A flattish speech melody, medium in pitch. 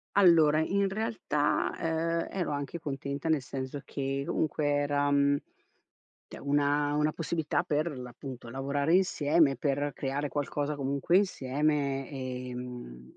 Yes: narrow, 2.1 semitones; medium, 145 Hz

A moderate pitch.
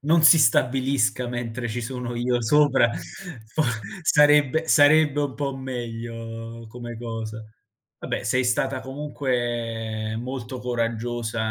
No: low, 120 Hz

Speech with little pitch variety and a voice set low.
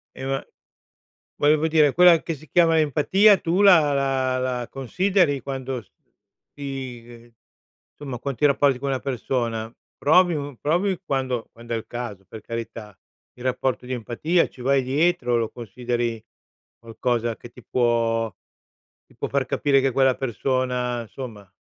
No: average, 3.4 semitones; low, 130 Hz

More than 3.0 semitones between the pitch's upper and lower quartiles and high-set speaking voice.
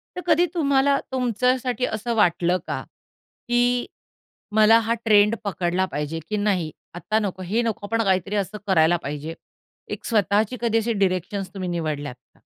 Yes: average, 4.5 semitones; high, 210 Hz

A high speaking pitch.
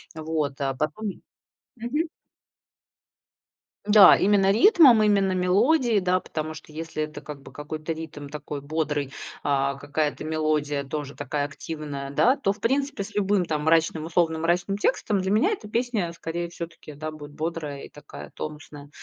No: medium, 160 Hz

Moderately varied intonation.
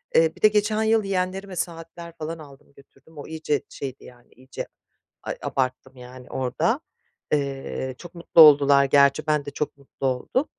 Yes: average, 3.8 semitones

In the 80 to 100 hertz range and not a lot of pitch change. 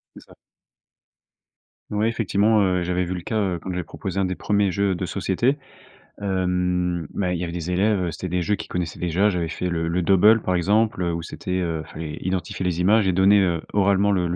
Yes: very low, 90 Hz; narrow, 2.3 semitones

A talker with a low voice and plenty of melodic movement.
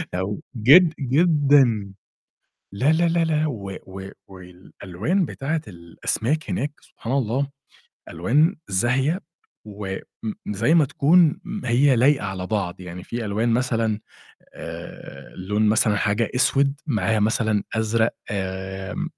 Yes: low, 115 Hz; wide, 6.2 semitones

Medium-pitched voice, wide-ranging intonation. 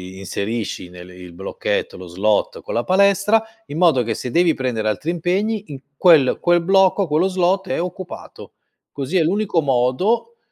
Yes: medium, 165 Hz; wide, 8.3 semitones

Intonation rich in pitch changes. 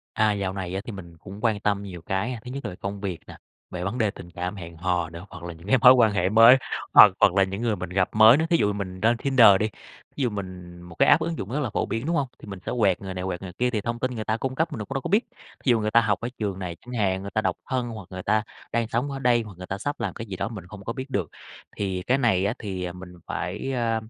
No: average, 4.1 semitones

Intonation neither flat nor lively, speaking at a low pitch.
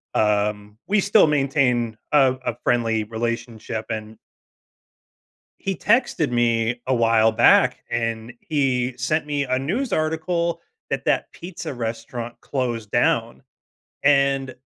Yes: average, 4.5 semitones; low, 125 Hz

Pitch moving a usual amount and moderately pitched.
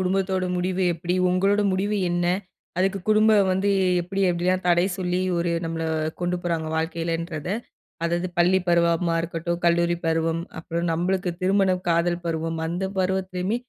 No: narrow, 1.8 semitones; medium, 175 Hz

